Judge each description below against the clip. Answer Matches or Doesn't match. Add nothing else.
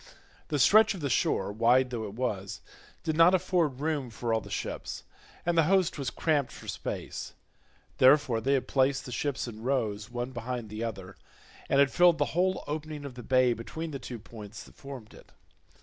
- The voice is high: Doesn't match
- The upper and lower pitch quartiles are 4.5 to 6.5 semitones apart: Matches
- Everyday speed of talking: Matches